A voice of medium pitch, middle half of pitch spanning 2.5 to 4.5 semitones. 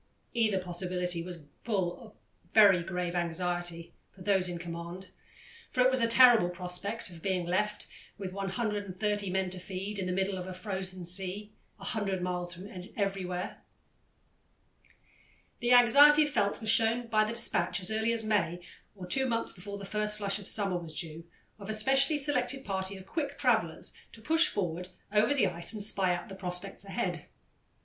No: high, 195 Hz; average, 3.3 semitones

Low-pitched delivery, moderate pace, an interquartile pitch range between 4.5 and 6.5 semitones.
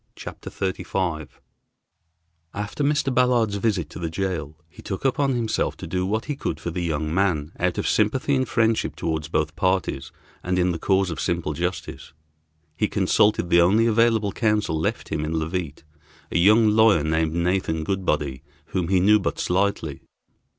Yes: very low, 90 Hz; average, 175 wpm; average, 4.8 semitones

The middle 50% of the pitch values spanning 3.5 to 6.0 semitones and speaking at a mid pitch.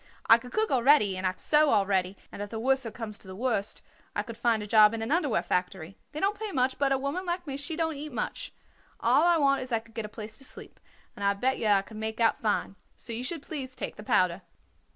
No: average, 4.9 semitones; high, 230 Hz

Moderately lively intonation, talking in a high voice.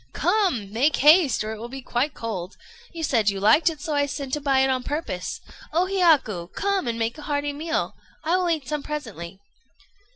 No: wide, 5.7 semitones; very high, 280 Hz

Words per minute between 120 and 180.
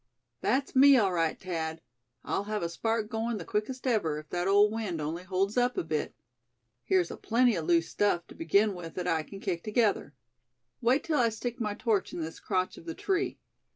No: fast, 205 wpm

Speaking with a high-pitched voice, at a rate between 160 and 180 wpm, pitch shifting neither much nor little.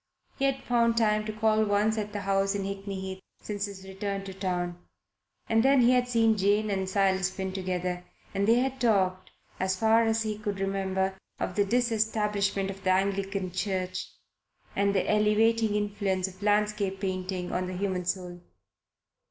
No: high, 200 Hz; average, 175 wpm; narrow, 2.2 semitones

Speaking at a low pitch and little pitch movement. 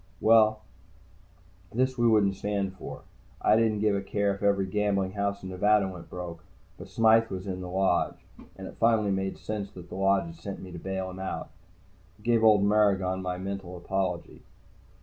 Yes: low, 100 Hz; narrow, 2.2 semitones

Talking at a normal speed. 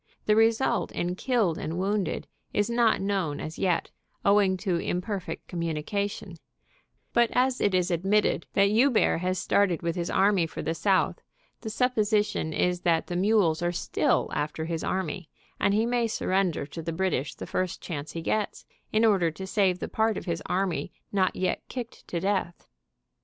Yes: average, 175 wpm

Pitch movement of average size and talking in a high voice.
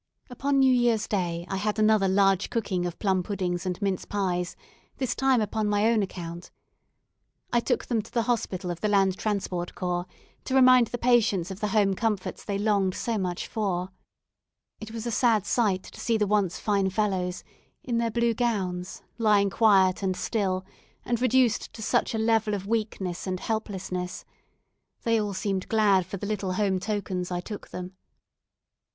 Yes: average, 3.1 semitones; high, 205 Hz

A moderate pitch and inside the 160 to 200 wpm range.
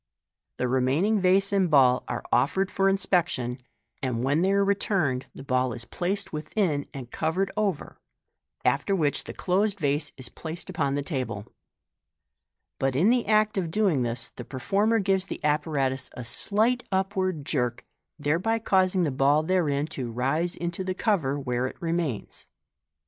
Yes: medium, 160 Hz; average, 165 wpm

